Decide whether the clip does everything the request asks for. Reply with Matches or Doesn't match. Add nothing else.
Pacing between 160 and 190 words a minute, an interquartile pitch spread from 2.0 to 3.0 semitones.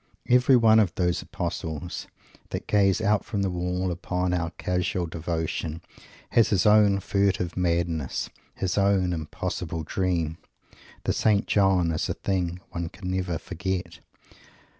Doesn't match